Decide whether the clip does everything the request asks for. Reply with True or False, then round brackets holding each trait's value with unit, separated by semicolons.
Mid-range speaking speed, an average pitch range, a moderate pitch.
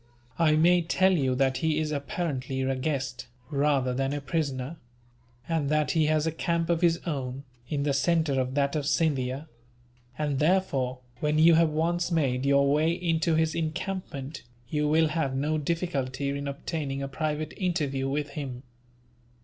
True (165 wpm; 3.0 semitones; 150 Hz)